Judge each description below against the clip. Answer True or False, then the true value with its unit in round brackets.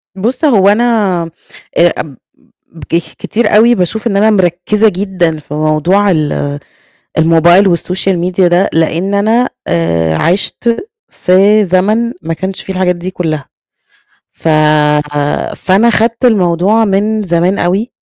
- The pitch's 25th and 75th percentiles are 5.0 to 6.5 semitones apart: False (3.9 semitones)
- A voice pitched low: False (185 Hz)